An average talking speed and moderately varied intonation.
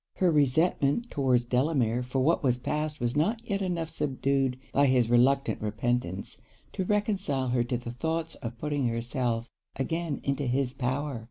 Yes: average, 160 wpm; average, 4.1 semitones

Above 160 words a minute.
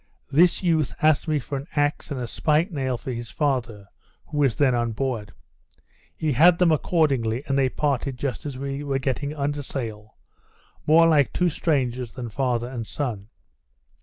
Yes: average, 175 wpm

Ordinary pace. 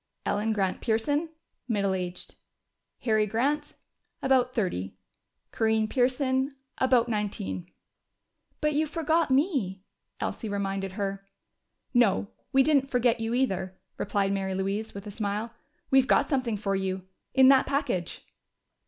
No: slow, 125 wpm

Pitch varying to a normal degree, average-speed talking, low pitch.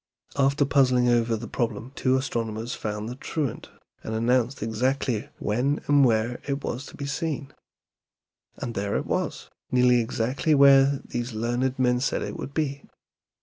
Yes: average, 3.1 semitones; average, 155 wpm; low, 125 Hz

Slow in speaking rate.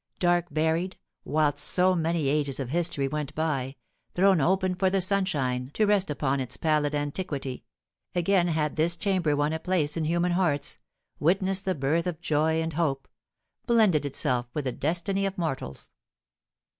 No: average, 160 wpm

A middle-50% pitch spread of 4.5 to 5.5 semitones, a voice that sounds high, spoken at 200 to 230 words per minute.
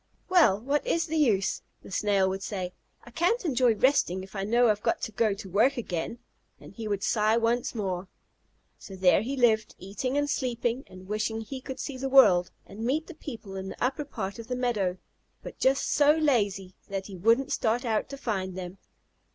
Yes: average, 5.1 semitones; high, 225 Hz; fast, 205 wpm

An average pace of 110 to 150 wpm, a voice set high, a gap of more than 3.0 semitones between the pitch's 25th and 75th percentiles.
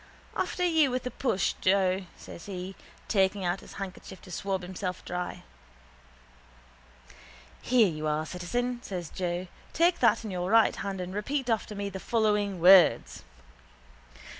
Yes: average, 145 wpm; high, 195 Hz; average, 3.9 semitones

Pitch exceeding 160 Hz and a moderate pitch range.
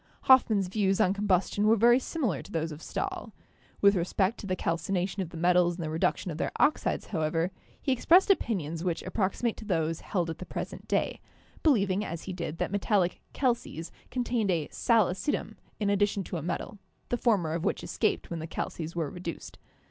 Yes: medium, 185 Hz; average, 4.1 semitones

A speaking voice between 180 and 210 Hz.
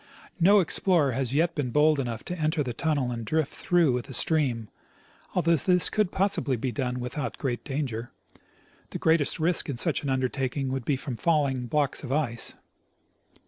No: medium, 140 Hz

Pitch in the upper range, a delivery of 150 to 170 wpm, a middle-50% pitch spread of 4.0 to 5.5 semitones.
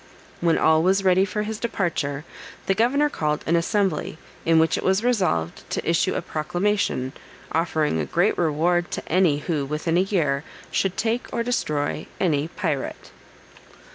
No: medium, 170 Hz; average, 160 wpm; average, 4.4 semitones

